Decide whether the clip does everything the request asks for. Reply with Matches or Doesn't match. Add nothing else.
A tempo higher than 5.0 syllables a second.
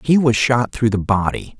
Doesn't match